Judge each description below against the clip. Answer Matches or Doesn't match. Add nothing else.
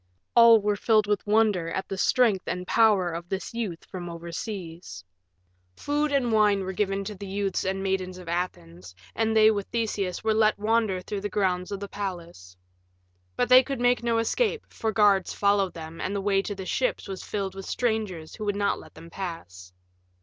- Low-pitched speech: Doesn't match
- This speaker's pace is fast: Doesn't match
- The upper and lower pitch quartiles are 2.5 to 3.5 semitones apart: Matches